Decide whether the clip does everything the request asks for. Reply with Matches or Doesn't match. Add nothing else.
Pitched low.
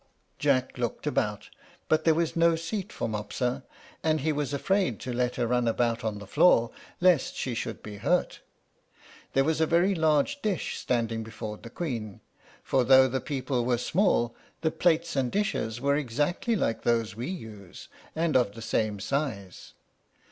Matches